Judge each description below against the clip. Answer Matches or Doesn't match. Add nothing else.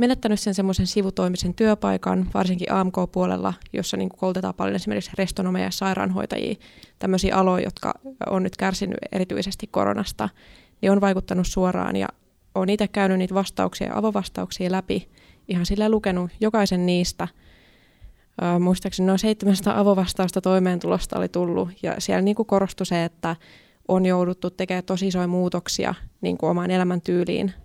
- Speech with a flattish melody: Matches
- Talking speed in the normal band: Matches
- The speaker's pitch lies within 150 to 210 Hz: Matches